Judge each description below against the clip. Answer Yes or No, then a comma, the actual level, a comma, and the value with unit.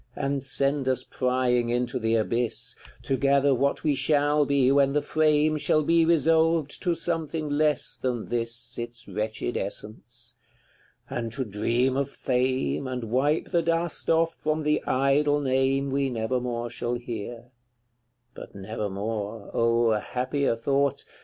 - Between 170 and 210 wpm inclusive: No, average, 145 wpm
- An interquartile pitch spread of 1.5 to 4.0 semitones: Yes, average, 3.7 semitones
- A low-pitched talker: Yes, low, 130 Hz